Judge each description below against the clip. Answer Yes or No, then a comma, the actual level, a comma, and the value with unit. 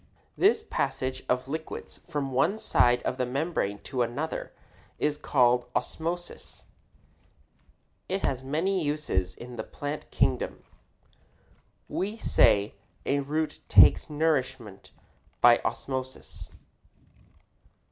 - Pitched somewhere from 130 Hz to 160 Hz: Yes, medium, 140 Hz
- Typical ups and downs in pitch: Yes, average, 4.0 semitones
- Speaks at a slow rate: Yes, slow, 105 wpm